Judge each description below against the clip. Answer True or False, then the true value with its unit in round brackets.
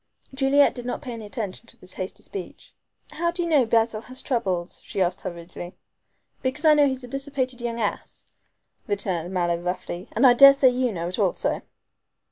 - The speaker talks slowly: False (180 wpm)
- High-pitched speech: True (235 Hz)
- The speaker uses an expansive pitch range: True (6.5 semitones)